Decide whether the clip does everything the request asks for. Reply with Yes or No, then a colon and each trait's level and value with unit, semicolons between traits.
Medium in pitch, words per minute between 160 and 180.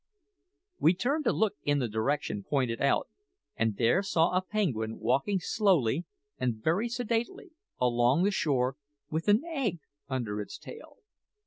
No: medium, 155 Hz; average, 145 wpm